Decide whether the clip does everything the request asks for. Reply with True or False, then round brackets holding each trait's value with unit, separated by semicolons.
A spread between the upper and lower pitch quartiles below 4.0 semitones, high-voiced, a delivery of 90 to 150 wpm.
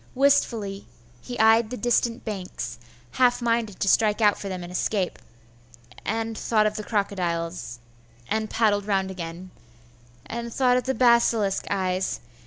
True (3.6 semitones; 215 Hz; 145 wpm)